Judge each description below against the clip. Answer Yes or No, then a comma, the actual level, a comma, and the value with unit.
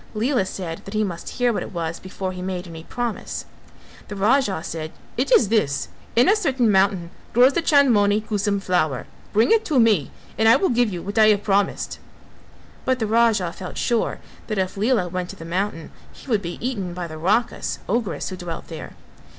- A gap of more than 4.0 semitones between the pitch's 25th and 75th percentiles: Yes, average, 4.6 semitones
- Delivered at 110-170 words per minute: No, average, 200 wpm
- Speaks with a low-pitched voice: No, high, 205 Hz